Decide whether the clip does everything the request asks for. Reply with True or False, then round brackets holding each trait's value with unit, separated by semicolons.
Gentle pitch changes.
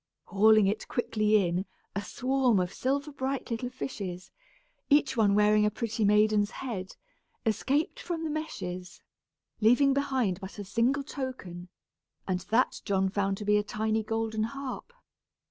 False (4.7 semitones)